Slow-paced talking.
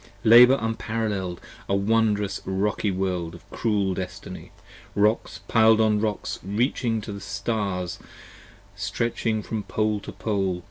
Yes: slow, 120 wpm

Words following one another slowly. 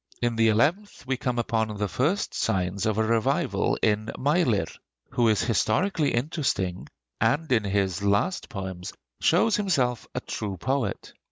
No: average, 150 wpm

